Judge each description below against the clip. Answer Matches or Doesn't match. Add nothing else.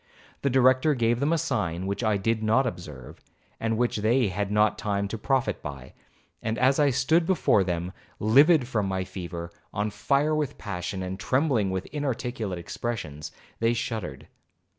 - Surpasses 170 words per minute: Doesn't match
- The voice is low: Matches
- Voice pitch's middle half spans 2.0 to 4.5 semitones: Doesn't match